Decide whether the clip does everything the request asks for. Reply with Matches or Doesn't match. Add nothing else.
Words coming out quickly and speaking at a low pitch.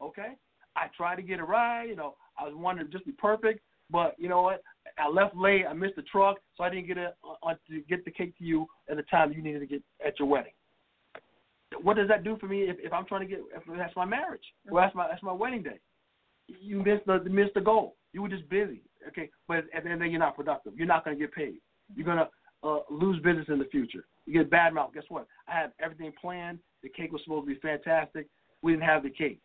Doesn't match